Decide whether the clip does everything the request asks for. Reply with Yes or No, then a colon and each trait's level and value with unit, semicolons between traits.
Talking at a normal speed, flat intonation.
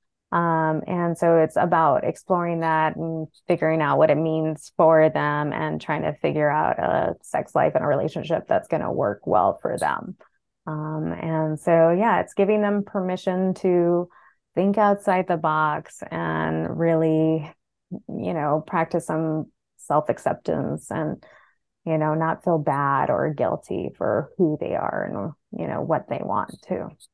Yes: average, 160 wpm; narrow, 2.2 semitones